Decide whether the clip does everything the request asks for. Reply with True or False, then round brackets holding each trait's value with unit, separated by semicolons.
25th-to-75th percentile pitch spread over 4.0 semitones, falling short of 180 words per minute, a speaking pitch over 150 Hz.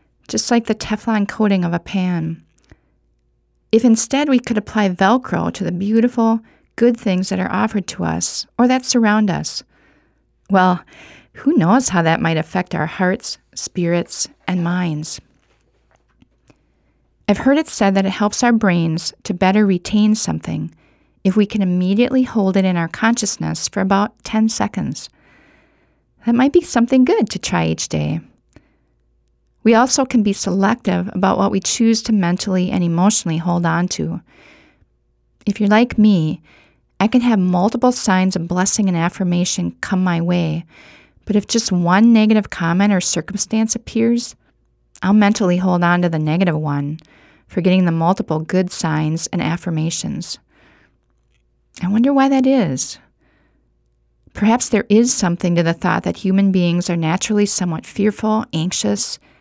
True (4.4 semitones; 155 wpm; 190 Hz)